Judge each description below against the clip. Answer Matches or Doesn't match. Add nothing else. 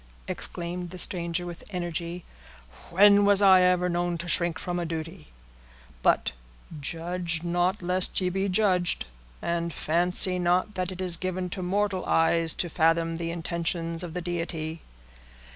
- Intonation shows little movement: Matches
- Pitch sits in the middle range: Matches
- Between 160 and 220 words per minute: Doesn't match